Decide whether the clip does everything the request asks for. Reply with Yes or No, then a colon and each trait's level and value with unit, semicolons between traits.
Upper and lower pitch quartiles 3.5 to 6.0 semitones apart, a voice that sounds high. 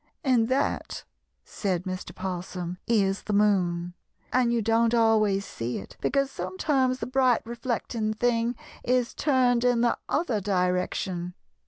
Yes: average, 4.8 semitones; high, 225 Hz